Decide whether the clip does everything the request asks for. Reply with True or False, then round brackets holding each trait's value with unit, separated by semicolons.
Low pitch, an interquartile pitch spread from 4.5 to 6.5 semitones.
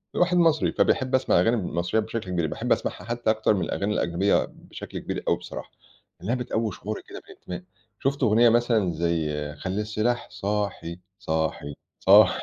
True (105 Hz; 5.0 semitones)